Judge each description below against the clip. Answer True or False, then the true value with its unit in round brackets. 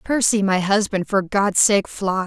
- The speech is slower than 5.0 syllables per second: True (4.2 syllables/s)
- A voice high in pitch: True (200 Hz)